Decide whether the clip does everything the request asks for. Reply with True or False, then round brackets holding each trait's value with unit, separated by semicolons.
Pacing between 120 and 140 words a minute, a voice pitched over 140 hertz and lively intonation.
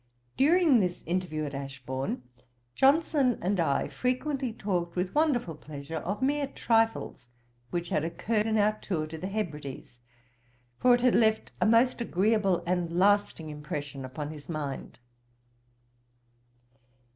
True (135 wpm; 185 Hz; 7.0 semitones)